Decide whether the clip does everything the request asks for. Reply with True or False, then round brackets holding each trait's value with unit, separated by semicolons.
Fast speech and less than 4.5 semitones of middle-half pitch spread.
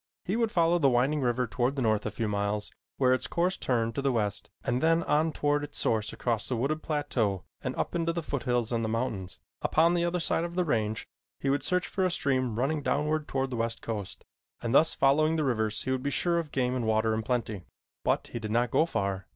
False (240 wpm; 5.4 semitones)